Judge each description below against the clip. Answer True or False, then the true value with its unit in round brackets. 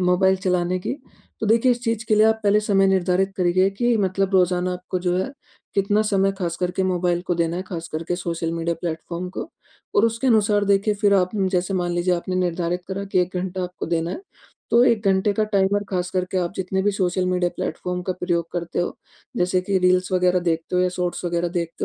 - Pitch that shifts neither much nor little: False (1.9 semitones)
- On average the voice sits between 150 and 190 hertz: True (185 Hz)